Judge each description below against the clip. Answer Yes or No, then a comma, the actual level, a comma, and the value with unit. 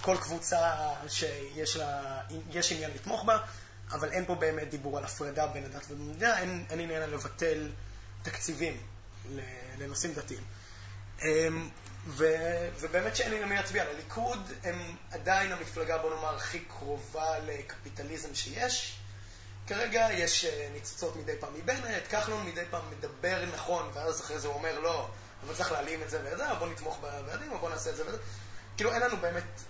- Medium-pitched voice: Yes, medium, 155 Hz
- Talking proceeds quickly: Yes, fast, 155 wpm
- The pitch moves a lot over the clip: Yes, wide, 8.9 semitones